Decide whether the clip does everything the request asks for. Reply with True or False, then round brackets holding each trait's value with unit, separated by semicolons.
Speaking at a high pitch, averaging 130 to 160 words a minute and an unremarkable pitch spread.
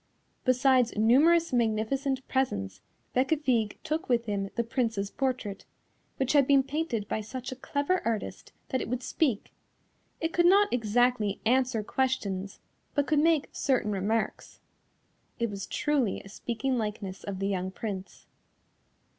True (245 Hz; 140 wpm; 4.4 semitones)